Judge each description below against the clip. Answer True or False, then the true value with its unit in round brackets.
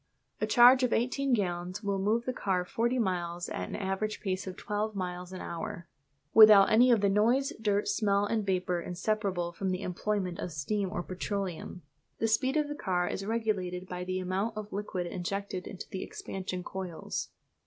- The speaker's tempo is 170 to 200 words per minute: True (185 wpm)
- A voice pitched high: True (195 Hz)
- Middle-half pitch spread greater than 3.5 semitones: False (3.0 semitones)